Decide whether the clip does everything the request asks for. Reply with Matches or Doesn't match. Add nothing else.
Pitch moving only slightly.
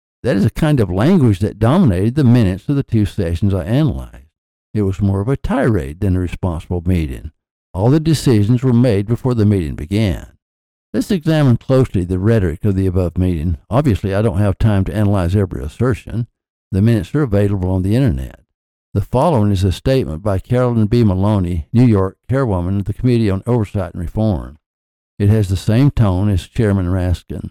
Doesn't match